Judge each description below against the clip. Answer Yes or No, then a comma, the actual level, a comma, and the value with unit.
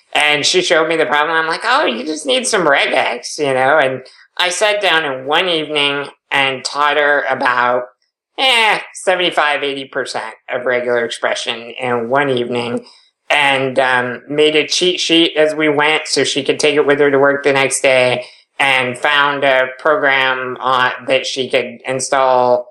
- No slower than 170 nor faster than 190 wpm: Yes, average, 175 wpm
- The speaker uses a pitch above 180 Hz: No, medium, 140 Hz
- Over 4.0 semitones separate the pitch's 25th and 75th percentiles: No, average, 2.8 semitones